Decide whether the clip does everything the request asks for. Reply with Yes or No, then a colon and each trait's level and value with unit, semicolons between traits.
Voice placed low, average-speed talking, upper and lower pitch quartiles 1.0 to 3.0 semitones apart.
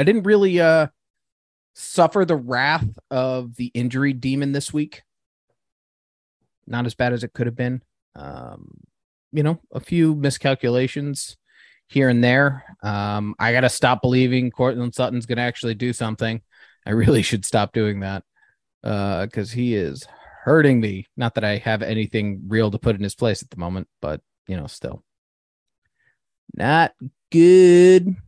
No: low, 120 Hz; average, 160 wpm; average, 4.4 semitones